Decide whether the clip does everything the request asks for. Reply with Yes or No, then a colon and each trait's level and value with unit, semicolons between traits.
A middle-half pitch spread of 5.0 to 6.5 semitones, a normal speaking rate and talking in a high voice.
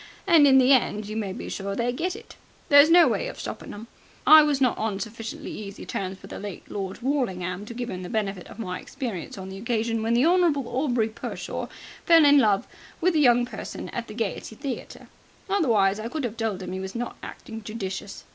No: wide, 5.4 semitones; fast, 220 wpm; high, 230 Hz